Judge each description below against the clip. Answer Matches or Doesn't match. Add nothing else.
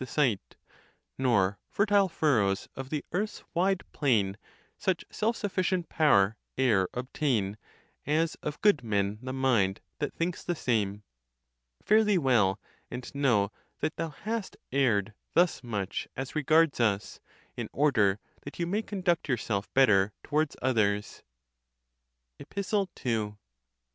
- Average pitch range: Doesn't match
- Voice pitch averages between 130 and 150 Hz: Matches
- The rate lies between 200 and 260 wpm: Doesn't match